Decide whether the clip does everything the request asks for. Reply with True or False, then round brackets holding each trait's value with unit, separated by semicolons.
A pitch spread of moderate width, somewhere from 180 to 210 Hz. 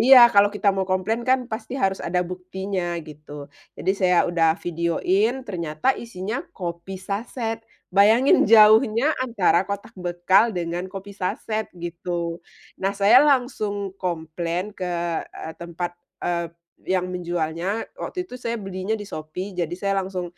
True (3.4 semitones; 190 Hz)